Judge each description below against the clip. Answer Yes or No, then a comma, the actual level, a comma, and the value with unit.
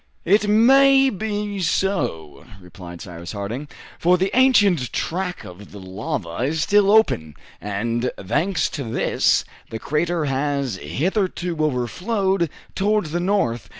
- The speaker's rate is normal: No, slow, 125 wpm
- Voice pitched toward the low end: No, medium, 155 Hz